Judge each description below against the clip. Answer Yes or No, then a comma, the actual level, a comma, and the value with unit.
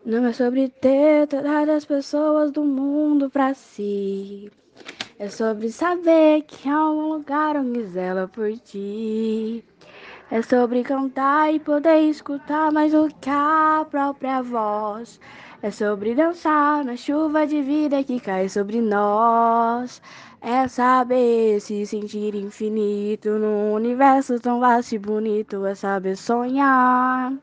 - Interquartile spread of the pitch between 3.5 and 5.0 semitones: No, wide, 5.4 semitones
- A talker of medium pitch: No, very high, 250 Hz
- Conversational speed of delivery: Yes, average, 130 wpm